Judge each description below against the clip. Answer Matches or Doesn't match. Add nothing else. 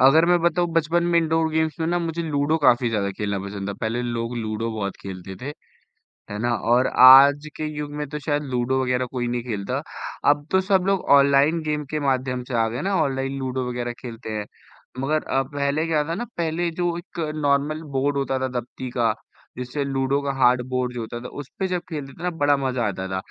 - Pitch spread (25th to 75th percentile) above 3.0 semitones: Matches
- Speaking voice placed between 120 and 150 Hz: Matches